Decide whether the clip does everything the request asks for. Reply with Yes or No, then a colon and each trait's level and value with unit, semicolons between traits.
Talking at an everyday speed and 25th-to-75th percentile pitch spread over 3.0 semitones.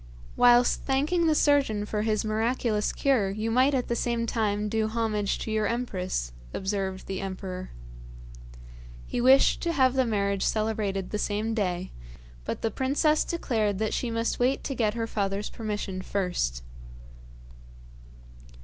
Yes: average, 150 wpm; average, 3.5 semitones